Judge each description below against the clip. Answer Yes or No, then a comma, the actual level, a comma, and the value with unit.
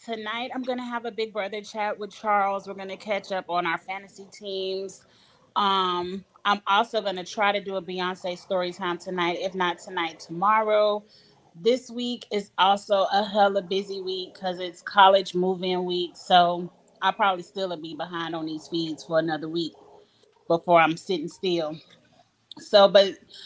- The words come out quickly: No, average, 170 wpm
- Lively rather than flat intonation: No, narrow, 2.5 semitones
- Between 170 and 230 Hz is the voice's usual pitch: Yes, high, 190 Hz